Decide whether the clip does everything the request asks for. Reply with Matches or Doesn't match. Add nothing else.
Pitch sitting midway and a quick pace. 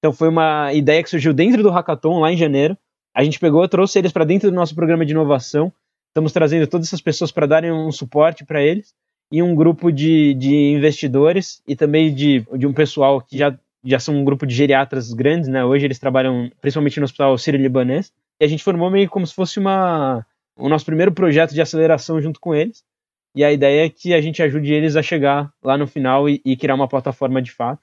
Matches